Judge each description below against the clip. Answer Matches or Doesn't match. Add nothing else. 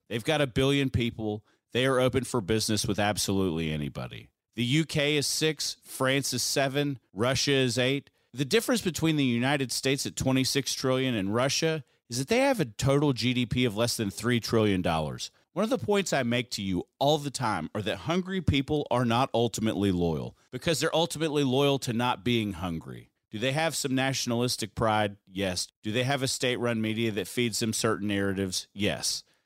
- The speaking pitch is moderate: Doesn't match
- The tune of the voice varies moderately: Matches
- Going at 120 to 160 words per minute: Doesn't match